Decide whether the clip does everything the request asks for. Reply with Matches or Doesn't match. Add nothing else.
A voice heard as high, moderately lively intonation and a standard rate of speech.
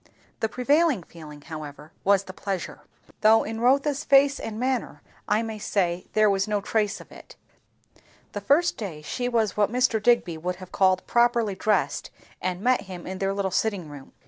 Matches